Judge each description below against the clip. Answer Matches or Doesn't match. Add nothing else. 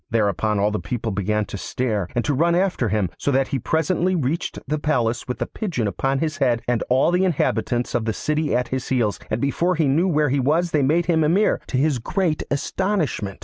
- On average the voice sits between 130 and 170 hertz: Matches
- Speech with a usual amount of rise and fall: Doesn't match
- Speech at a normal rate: Doesn't match